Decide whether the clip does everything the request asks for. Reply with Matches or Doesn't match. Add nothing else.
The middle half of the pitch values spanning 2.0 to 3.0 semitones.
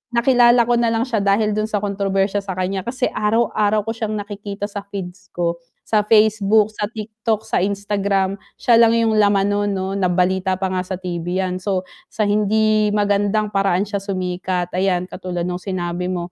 Matches